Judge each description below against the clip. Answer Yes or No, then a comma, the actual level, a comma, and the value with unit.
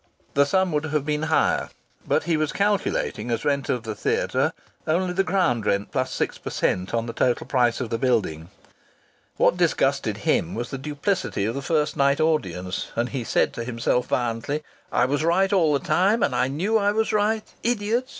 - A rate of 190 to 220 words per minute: Yes, average, 200 wpm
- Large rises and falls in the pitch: Yes, wide, 7.4 semitones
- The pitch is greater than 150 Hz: No, medium, 145 Hz